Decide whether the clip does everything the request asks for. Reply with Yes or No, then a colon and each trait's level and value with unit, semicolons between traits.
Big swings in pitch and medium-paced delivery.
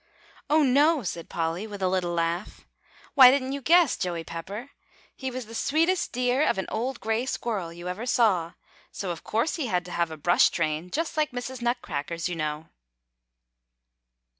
Yes: wide, 7.2 semitones; average, 180 wpm